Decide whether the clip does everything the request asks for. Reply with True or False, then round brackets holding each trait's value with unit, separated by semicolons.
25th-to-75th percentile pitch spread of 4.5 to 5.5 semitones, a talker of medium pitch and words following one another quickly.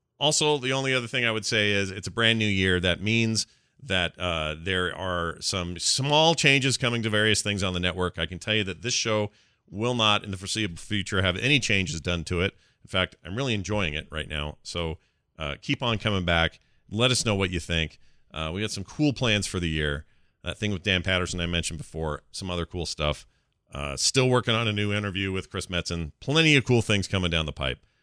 False (4.8 semitones; 100 Hz; 230 wpm)